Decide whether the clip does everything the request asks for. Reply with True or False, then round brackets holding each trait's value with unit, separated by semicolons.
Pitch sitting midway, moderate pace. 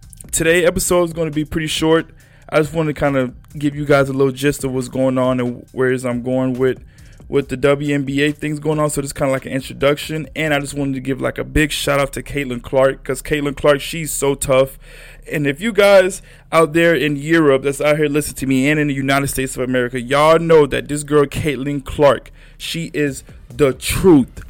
False (145 Hz; 230 wpm)